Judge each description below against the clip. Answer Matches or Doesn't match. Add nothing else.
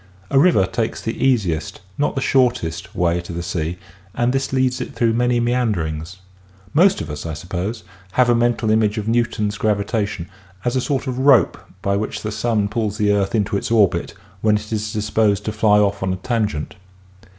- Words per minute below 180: Doesn't match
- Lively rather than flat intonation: Doesn't match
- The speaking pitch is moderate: Doesn't match